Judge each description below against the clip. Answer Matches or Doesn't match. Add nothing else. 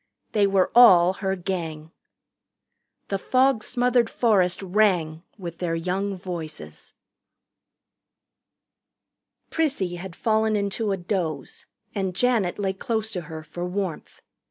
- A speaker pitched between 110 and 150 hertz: Doesn't match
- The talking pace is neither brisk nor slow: Doesn't match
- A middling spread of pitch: Matches